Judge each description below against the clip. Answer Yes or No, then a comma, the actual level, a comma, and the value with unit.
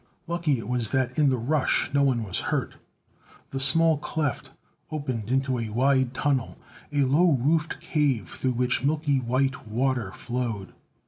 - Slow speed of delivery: No, average, 155 wpm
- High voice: No, low, 130 Hz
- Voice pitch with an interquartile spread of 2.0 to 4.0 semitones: Yes, average, 3.0 semitones